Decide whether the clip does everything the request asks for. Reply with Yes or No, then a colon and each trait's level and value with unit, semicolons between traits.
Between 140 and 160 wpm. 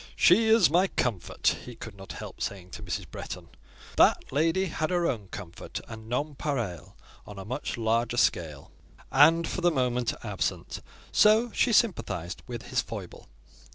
Yes: average, 155 wpm